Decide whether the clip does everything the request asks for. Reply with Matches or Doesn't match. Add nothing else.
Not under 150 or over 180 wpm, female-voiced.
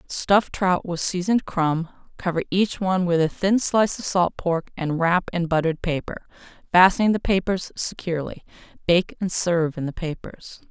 Matches